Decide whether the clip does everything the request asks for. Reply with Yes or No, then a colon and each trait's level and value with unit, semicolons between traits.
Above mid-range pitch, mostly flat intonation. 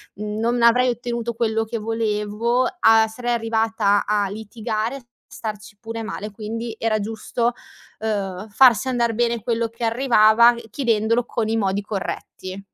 Yes: high, 225 Hz; narrow, 1.9 semitones